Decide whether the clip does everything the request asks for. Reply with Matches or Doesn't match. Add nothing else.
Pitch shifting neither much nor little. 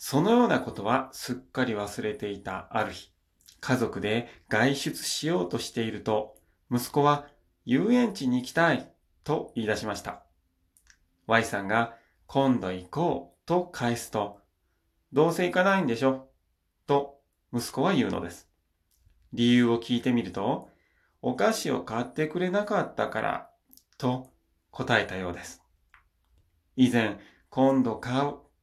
Doesn't match